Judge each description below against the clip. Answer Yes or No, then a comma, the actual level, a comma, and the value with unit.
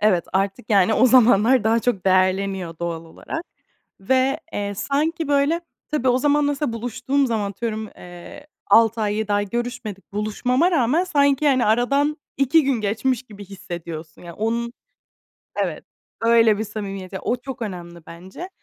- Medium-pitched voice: No, high, 225 Hz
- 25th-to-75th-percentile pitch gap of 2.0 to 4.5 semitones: No, average, 5.2 semitones